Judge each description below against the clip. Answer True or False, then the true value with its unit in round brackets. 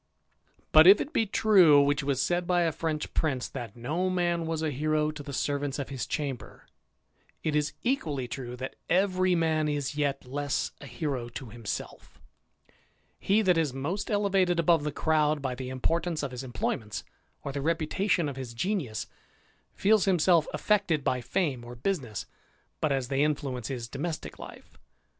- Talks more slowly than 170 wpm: False (175 wpm)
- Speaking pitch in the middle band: True (150 Hz)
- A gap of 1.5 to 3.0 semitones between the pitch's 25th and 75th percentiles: False (4.5 semitones)